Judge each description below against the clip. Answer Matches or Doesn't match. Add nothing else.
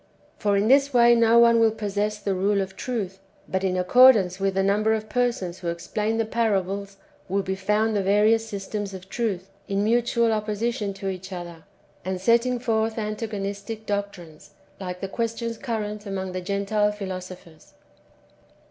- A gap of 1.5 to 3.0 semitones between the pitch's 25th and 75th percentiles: Matches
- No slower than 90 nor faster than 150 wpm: Doesn't match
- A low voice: Doesn't match